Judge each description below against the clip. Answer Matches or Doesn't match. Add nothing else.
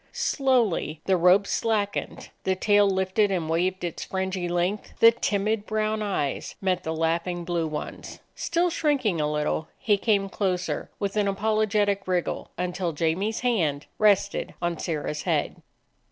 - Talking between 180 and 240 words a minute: Doesn't match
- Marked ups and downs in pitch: Doesn't match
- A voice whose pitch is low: Doesn't match